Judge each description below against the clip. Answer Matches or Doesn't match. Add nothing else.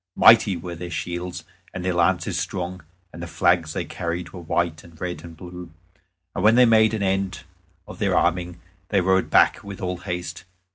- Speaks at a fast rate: Doesn't match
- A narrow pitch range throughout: Matches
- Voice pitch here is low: Matches